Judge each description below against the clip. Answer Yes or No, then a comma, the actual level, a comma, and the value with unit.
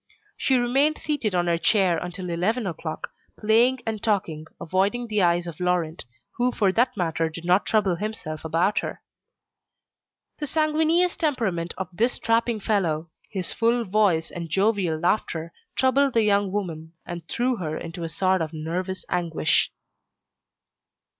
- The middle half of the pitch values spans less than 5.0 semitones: No, average, 5.3 semitones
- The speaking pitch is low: No, high, 190 Hz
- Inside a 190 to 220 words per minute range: No, average, 150 wpm